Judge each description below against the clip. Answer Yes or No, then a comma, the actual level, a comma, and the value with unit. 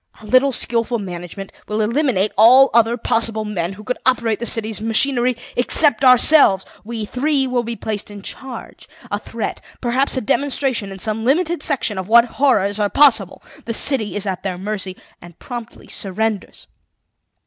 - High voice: Yes, high, 225 Hz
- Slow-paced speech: No, average, 165 wpm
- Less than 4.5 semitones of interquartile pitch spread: Yes, average, 3.6 semitones